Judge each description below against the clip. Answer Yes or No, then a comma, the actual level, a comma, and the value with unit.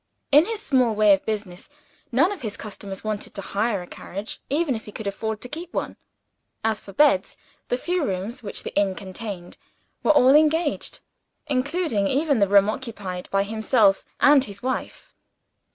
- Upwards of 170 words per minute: Yes, average, 180 wpm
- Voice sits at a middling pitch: No, high, 220 Hz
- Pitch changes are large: Yes, wide, 5.9 semitones